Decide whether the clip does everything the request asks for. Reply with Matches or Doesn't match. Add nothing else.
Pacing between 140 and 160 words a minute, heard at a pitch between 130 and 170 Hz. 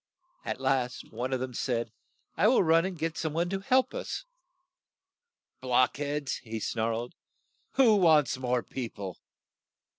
Matches